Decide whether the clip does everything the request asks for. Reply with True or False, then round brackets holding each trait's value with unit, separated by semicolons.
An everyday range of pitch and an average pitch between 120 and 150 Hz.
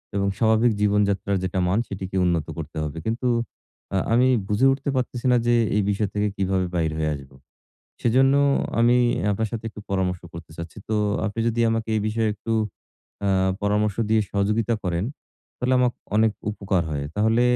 False (3.3 semitones; 105 Hz)